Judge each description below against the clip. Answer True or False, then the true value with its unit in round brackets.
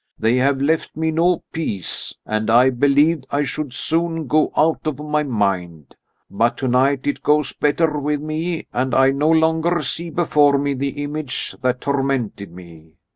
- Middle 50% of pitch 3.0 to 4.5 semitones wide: True (3.5 semitones)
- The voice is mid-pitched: True (145 Hz)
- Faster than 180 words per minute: False (165 wpm)